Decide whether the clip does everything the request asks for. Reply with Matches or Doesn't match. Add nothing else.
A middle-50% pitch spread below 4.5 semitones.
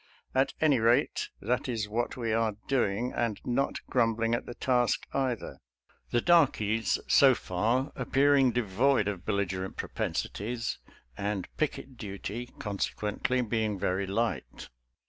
Matches